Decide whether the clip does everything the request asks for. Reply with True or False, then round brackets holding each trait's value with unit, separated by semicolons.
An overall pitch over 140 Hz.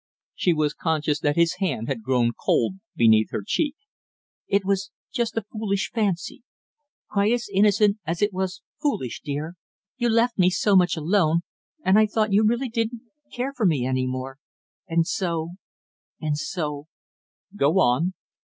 True (185 Hz)